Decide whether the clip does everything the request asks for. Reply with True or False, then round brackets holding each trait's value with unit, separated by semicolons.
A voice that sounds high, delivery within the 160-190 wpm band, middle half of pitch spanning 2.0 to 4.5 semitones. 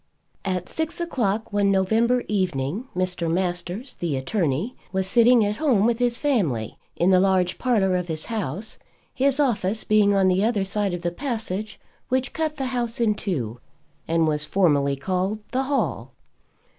False (200 Hz; 165 wpm; 5.0 semitones)